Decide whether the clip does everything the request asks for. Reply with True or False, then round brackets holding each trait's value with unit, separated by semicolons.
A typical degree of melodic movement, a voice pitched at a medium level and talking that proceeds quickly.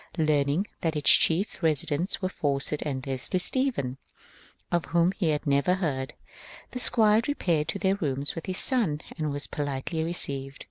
False (4.5 semitones; 155 Hz; 170 wpm)